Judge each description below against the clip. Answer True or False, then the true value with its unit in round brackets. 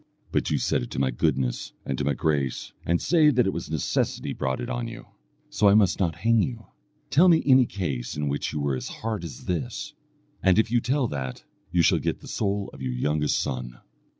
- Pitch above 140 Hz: False (85 Hz)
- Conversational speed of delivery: False (225 wpm)